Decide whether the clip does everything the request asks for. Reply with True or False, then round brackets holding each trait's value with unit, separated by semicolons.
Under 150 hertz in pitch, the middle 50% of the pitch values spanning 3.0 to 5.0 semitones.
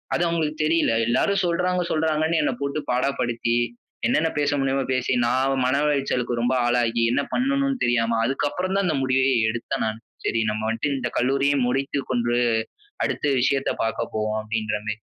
True (135 Hz; 4.5 semitones)